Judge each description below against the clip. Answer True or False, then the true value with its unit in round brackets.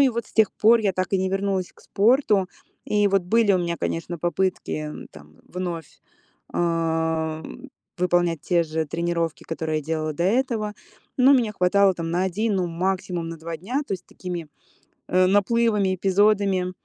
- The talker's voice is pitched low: False (185 Hz)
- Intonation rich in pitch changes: False (3.5 semitones)